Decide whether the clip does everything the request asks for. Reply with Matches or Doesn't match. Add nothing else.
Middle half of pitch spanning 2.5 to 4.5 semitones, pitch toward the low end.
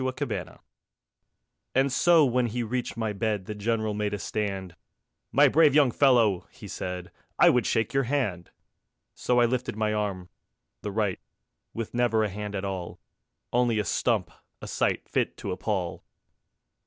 Matches